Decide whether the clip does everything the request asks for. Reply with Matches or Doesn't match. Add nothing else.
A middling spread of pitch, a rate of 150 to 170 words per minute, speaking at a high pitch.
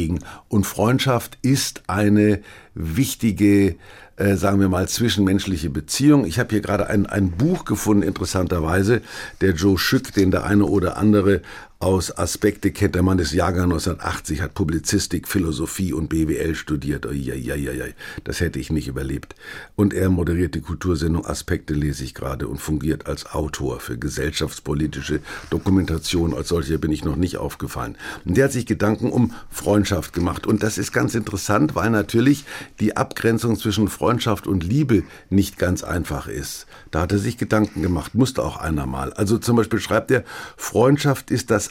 Doesn't match